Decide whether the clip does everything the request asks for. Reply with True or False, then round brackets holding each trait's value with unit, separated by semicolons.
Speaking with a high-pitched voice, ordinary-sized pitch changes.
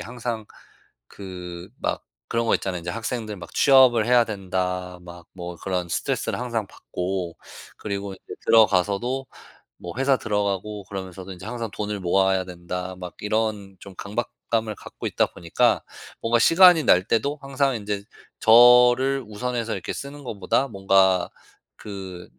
False (105 Hz; 4.3 semitones)